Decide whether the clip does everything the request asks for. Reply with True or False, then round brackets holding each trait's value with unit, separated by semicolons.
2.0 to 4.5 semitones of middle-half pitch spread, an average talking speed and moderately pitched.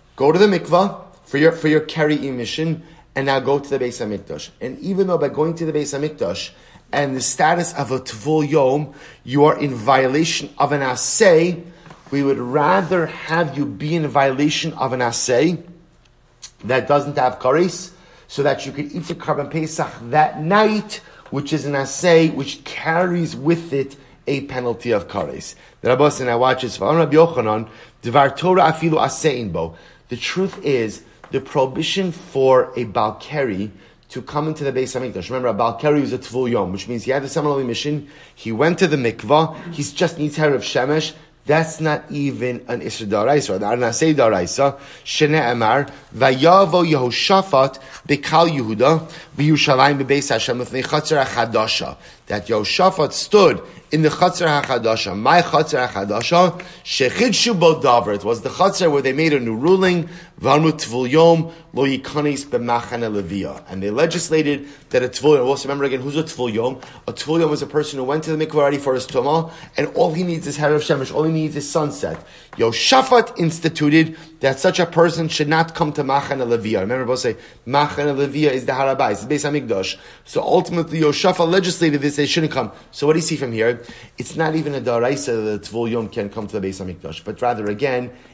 True (4.0 semitones; 170 wpm; 145 Hz)